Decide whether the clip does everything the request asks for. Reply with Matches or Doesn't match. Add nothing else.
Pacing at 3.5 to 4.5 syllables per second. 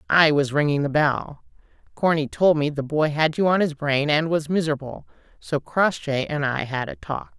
Doesn't match